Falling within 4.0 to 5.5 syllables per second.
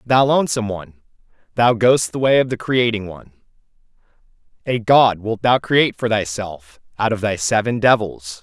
Yes: 5.3 syllables/s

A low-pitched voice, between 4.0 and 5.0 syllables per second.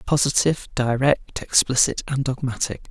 Yes: low, 130 Hz; 4.9 syllables/s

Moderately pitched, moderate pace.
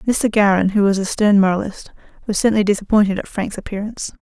No: high, 205 Hz; average, 185 wpm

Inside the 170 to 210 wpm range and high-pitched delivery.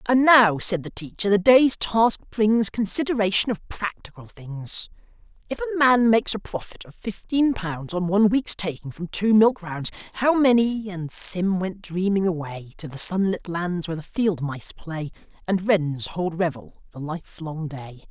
Yes: average, 175 wpm; high, 195 Hz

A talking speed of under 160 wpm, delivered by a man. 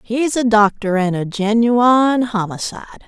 No: slow, 135 wpm; female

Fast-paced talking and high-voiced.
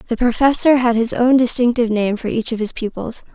Yes: fast, 215 wpm; high, 235 Hz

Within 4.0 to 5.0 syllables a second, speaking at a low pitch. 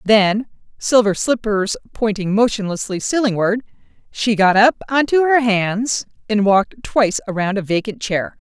No: 4.6 syllables/s; high, 215 Hz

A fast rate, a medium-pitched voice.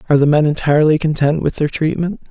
Yes: fast, 210 wpm; medium, 155 Hz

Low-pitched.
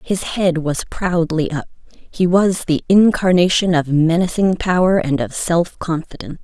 No: medium, 170 Hz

